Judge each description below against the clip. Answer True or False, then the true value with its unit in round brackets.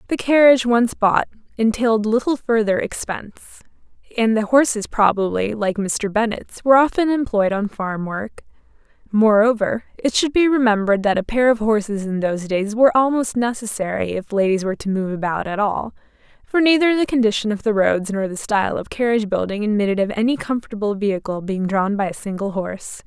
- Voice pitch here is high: True (220 Hz)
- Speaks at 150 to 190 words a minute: True (180 wpm)